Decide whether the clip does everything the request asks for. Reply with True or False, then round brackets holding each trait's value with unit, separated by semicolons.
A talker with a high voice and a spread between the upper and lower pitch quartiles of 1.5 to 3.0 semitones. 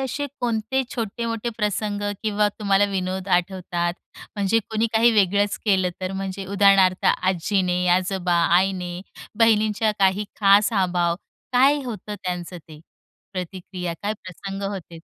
True (195 Hz; 2.6 semitones)